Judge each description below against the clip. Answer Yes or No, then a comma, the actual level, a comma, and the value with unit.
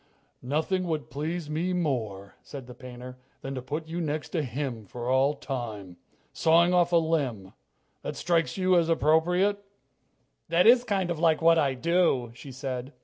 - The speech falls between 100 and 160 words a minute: No, average, 170 wpm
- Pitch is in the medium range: Yes, medium, 155 Hz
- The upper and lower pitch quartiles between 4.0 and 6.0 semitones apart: Yes, average, 5.0 semitones